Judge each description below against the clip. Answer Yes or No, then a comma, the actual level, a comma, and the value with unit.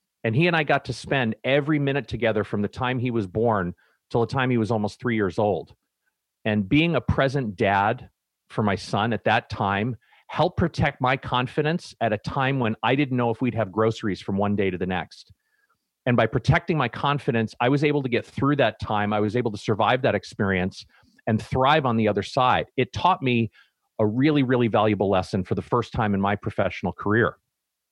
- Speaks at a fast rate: Yes, fast, 215 wpm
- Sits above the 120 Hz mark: No, low, 115 Hz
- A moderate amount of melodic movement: Yes, average, 4.2 semitones